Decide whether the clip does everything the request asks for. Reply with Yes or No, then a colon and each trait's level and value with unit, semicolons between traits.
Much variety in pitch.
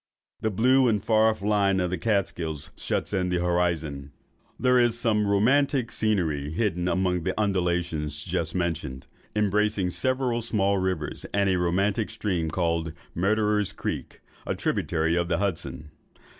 No: average, 3.9 semitones